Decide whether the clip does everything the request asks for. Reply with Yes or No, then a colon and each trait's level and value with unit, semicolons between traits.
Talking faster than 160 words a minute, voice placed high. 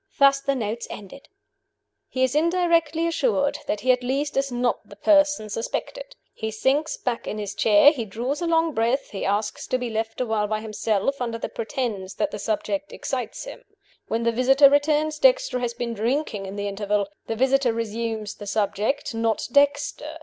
Yes: average, 185 wpm; high, 245 Hz